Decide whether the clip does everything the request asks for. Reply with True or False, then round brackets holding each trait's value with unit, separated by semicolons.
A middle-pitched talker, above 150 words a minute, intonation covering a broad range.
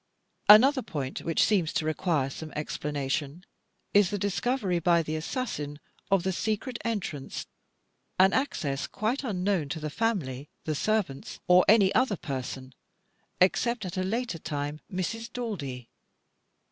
False (180 Hz; 135 wpm; 6.5 semitones)